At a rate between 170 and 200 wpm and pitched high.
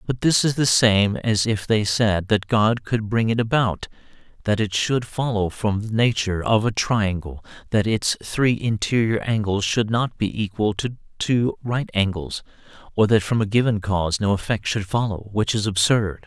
No: average, 190 wpm; low, 105 Hz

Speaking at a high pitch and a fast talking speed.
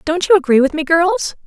Yes: very high, 330 Hz; fast, 245 wpm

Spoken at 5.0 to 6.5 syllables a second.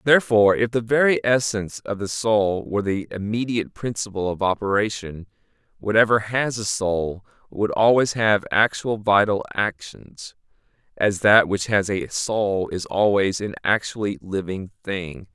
No: 4.5 syllables/s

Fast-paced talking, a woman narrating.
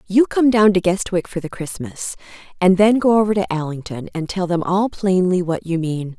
Yes: fast, 215 wpm; female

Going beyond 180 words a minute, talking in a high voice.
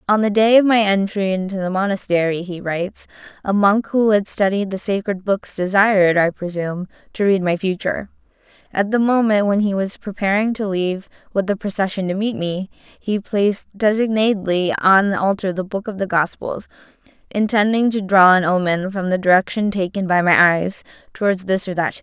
Yes: average, 190 wpm; high, 195 Hz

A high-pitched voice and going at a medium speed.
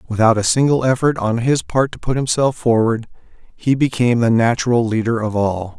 No: low, 120 Hz; average, 185 wpm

